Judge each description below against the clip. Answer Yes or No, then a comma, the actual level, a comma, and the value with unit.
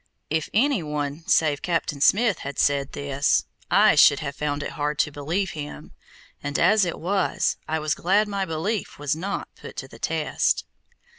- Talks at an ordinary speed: Yes, average, 175 wpm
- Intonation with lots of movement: No, average, 4.8 semitones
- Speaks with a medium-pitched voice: Yes, medium, 155 Hz